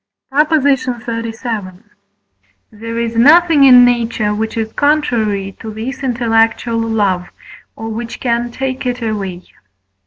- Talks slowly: Yes, slow, 120 wpm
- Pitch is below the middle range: No, high, 230 Hz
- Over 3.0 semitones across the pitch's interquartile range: No, narrow, 2.5 semitones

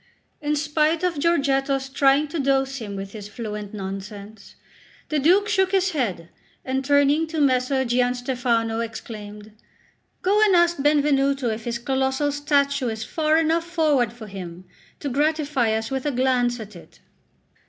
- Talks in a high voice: Yes, very high, 270 Hz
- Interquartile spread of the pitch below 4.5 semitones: No, average, 4.9 semitones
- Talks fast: No, average, 155 wpm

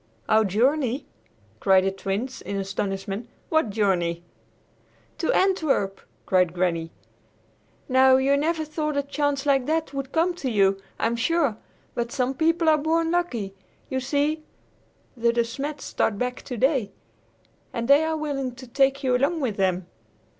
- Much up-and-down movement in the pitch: Yes, wide, 6.3 semitones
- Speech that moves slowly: No, average, 150 wpm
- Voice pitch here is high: Yes, very high, 260 Hz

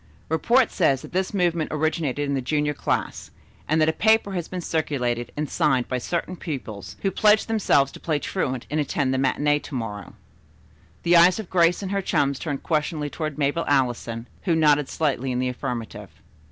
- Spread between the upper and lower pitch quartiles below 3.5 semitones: No, average, 4.5 semitones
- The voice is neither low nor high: Yes, medium, 150 Hz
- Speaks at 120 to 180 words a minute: No, average, 190 wpm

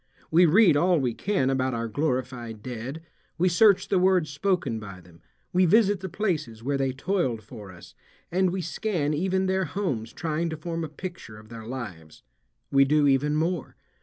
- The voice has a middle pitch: Yes, medium, 150 Hz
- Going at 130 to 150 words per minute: No, average, 185 wpm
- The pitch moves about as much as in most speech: No, wide, 7.0 semitones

